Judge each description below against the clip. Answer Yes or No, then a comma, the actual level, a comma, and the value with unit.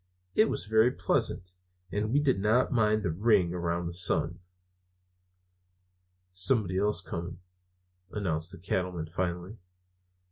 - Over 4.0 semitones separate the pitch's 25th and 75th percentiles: No, average, 3.7 semitones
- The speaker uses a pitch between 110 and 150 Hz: No, very low, 95 Hz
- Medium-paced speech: No, slow, 120 wpm